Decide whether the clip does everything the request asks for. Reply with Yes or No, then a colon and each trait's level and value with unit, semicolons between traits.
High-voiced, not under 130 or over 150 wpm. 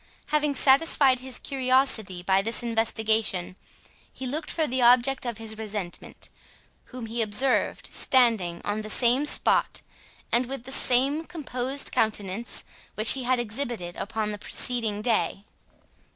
Yes: high, 240 Hz; slow, 135 wpm